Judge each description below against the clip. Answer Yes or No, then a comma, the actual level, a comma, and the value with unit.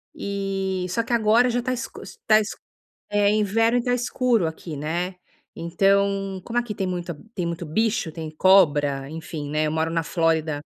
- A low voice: No, high, 190 Hz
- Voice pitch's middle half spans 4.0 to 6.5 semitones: Yes, average, 4.8 semitones